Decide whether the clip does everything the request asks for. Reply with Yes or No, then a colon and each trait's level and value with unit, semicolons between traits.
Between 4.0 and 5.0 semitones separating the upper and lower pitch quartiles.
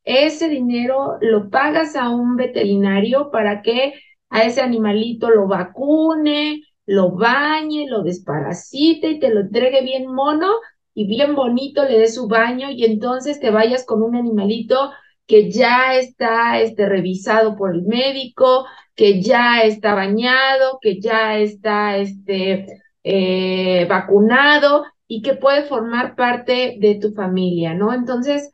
Yes: average, 4.3 semitones